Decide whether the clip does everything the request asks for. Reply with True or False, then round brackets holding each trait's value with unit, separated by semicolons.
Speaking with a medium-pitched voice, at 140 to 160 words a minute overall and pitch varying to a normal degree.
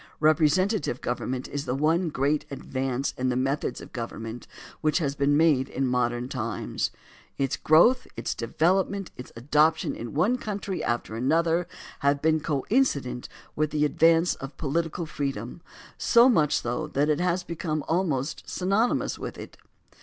True (150 Hz; 155 wpm; 4.3 semitones)